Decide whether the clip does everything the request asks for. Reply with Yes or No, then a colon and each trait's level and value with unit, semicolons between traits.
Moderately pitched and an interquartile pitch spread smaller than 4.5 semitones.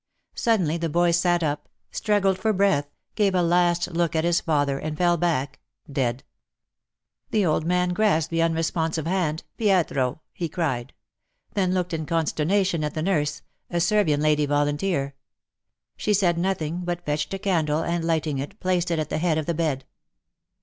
Yes: medium, 165 Hz; average, 3.0 semitones